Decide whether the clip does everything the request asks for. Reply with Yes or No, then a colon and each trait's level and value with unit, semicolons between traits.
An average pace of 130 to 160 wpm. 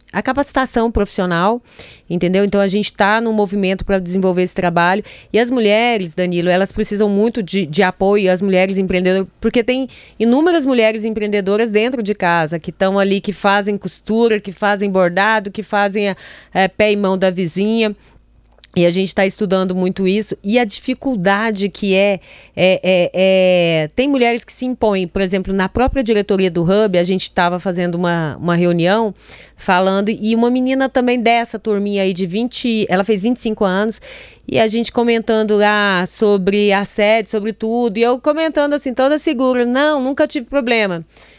No: average, 175 wpm